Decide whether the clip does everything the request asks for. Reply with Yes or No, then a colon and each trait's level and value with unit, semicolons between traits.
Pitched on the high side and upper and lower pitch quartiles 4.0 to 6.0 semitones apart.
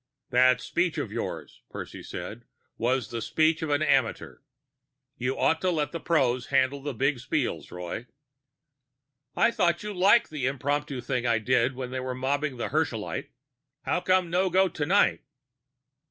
No: medium, 140 Hz; average, 4.6 semitones